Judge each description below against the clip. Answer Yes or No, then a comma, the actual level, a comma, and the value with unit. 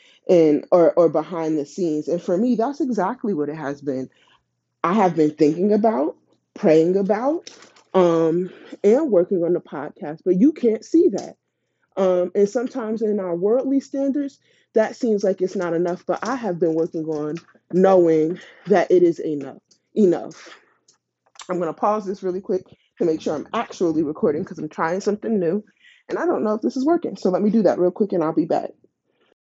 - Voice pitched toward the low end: No, high, 190 Hz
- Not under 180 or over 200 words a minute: Yes, average, 195 wpm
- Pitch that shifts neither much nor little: No, wide, 6.3 semitones